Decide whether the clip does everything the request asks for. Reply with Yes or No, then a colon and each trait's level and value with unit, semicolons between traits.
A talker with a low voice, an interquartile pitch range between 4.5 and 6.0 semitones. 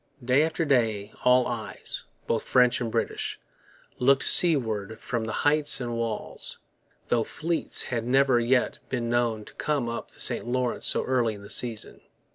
No: low, 120 Hz; narrow, 2.6 semitones